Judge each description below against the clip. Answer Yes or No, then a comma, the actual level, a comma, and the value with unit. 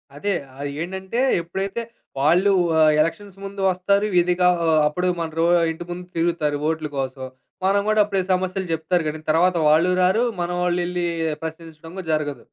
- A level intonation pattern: No, average, 3.0 semitones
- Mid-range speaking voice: Yes, medium, 175 Hz